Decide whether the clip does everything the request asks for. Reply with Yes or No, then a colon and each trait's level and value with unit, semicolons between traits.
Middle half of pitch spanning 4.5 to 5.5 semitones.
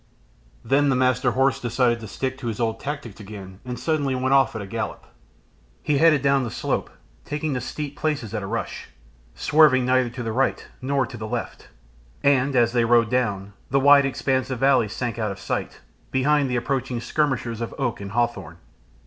No: average, 3.1 semitones